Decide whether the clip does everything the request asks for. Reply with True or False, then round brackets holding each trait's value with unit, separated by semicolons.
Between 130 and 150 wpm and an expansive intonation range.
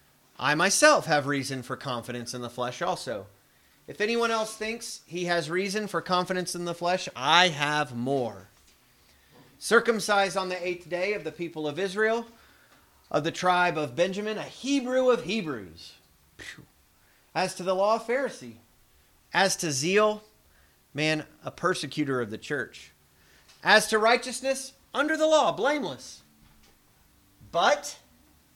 True (140 wpm; 9.0 semitones)